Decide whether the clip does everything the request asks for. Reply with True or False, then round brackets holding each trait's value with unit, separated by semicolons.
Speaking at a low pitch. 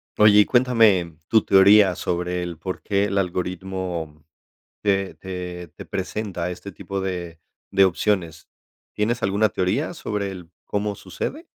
True (95 Hz)